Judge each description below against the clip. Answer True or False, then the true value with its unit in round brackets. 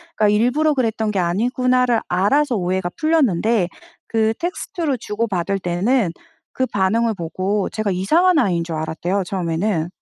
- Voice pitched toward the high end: True (210 Hz)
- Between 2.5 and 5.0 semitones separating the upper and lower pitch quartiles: False (5.5 semitones)